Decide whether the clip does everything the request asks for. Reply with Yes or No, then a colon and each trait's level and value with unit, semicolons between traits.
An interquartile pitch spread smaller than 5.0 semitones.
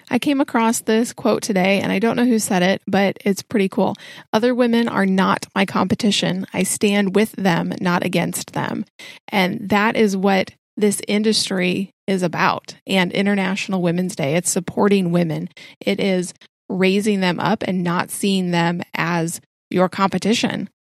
Yes: average, 2.7 semitones